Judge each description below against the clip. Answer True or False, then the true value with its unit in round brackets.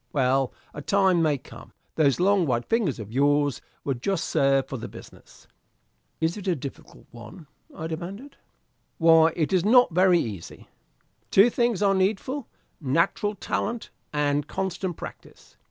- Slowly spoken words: False (150 wpm)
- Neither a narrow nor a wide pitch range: False (5.7 semitones)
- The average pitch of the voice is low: False (165 Hz)